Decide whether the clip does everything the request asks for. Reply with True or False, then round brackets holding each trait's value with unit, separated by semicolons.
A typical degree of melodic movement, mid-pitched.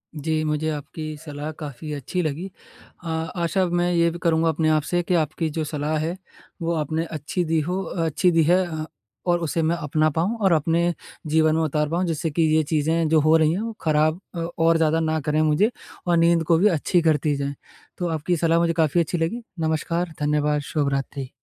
False (1.8 semitones; 160 Hz)